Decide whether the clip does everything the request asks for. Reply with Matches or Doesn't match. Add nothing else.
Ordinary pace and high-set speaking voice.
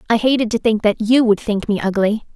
Doesn't match